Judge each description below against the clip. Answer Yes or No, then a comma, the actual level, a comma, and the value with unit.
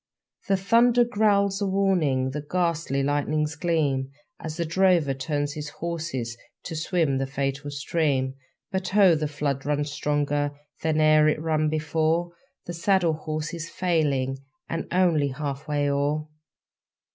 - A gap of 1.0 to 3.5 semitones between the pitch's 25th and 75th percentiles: Yes, average, 3.0 semitones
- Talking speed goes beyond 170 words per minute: No, average, 145 wpm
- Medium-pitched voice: Yes, medium, 155 Hz